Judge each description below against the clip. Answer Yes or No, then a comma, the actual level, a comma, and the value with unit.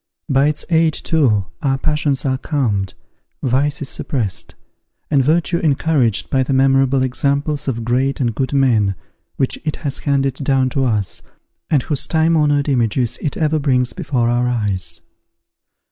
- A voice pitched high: No, low, 135 Hz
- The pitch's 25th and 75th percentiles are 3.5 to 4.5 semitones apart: No, average, 3.0 semitones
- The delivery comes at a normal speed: Yes, average, 155 wpm